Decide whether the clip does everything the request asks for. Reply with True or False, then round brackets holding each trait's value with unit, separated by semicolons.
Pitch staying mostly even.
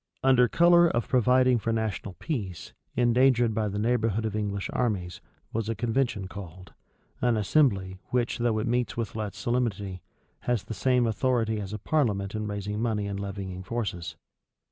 False (3.4 semitones)